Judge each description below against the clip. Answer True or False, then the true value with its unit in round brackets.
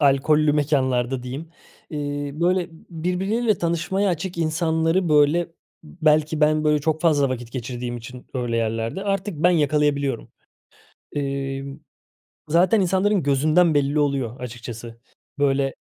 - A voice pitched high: False (150 Hz)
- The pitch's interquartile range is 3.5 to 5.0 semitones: True (3.8 semitones)